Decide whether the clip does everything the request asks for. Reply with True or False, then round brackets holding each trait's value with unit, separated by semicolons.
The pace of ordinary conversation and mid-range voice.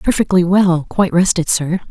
True (155 wpm; 180 Hz)